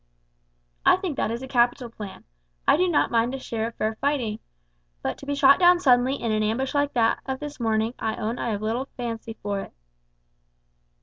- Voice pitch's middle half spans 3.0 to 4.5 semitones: Yes, average, 3.8 semitones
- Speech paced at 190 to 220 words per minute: Yes, fast, 205 wpm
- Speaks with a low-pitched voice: No, high, 240 Hz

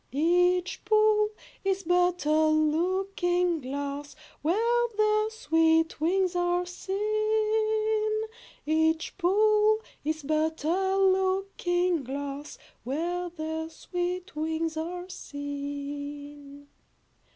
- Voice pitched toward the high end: Yes, very high, 350 Hz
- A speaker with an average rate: No, slow, 90 wpm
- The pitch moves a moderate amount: Yes, average, 3.9 semitones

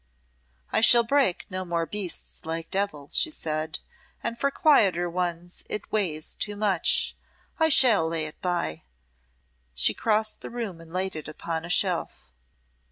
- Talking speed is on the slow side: No, average, 155 wpm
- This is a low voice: No, medium, 180 Hz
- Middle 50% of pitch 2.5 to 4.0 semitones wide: No, average, 4.7 semitones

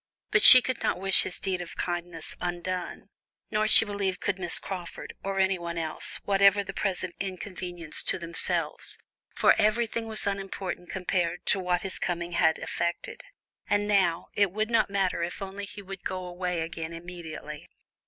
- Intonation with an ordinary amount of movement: No, narrow, 2.3 semitones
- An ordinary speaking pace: Yes, average, 165 wpm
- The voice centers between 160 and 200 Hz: Yes, medium, 185 Hz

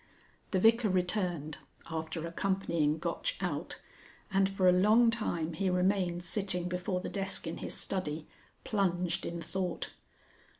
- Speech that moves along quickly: No, slow, 135 wpm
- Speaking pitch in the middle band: Yes, medium, 180 Hz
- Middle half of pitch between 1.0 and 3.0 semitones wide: Yes, narrow, 2.4 semitones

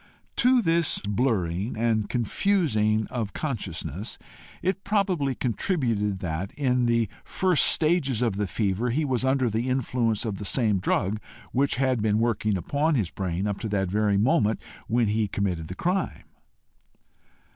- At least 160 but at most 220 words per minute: No, average, 150 wpm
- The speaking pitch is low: Yes, low, 115 Hz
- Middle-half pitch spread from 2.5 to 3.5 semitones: No, average, 4.9 semitones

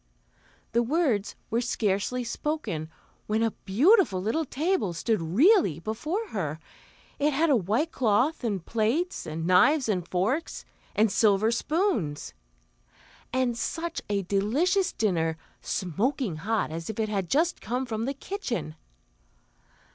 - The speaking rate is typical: No, slow, 130 wpm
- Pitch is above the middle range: Yes, high, 225 Hz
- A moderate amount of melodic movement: No, wide, 7.4 semitones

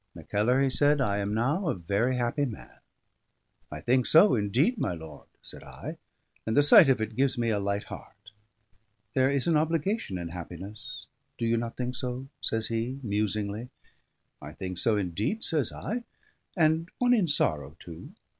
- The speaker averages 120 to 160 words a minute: No, average, 175 wpm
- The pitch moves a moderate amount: No, wide, 6.0 semitones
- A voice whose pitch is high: No, low, 115 Hz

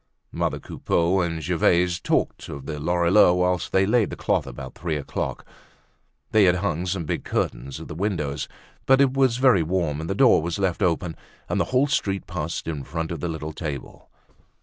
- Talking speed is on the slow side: No, average, 195 wpm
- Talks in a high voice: No, very low, 85 Hz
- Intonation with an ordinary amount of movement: Yes, average, 3.6 semitones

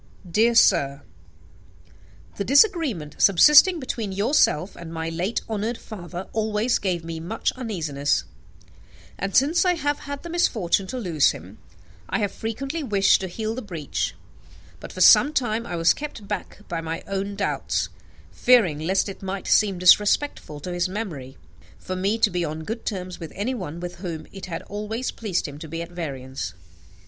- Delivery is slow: No, average, 170 wpm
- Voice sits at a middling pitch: No, high, 195 Hz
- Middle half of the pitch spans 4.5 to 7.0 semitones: Yes, average, 5.2 semitones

